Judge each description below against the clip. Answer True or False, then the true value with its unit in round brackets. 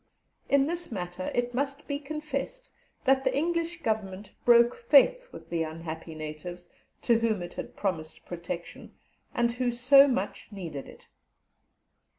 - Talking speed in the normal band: True (145 wpm)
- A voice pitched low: False (235 Hz)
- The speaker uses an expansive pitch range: True (8.0 semitones)